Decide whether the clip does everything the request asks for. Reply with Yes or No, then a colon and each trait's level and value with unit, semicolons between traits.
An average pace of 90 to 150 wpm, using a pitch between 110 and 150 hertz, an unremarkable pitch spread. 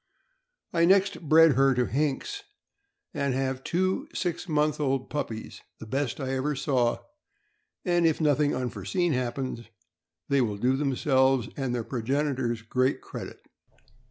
Yes: slow, 135 wpm; low, 135 Hz; average, 3.1 semitones